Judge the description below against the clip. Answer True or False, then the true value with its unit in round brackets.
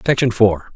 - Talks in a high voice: False (110 Hz)